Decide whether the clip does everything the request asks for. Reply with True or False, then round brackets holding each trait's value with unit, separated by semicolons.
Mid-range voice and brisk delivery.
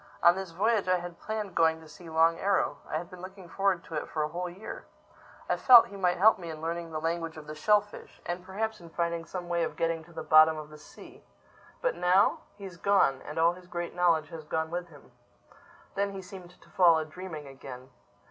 True (170 Hz; 225 wpm)